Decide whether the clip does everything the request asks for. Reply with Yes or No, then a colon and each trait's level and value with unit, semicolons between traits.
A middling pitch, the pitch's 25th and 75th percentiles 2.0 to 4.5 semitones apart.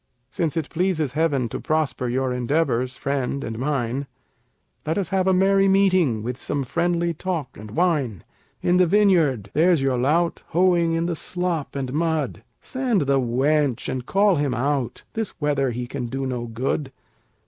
No: medium, 145 Hz; average, 5.1 semitones